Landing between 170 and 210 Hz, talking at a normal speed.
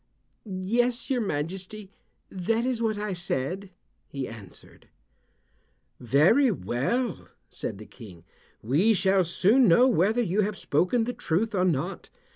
No: high, 190 Hz; slow, 130 wpm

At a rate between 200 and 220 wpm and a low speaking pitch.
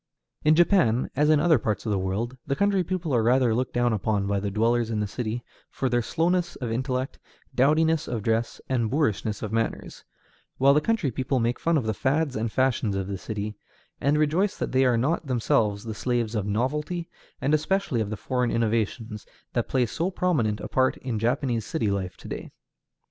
Yes: fast, 205 wpm; low, 125 Hz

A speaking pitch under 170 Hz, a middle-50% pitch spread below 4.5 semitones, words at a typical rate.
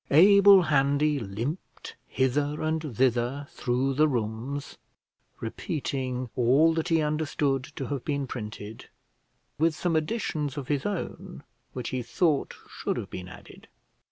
No: medium, 140 Hz; average, 3.7 semitones; slow, 130 wpm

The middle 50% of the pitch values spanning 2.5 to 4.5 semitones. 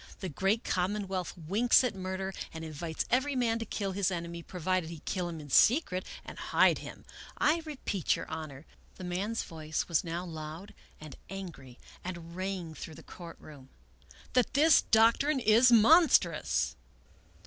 No: average, 5.2 semitones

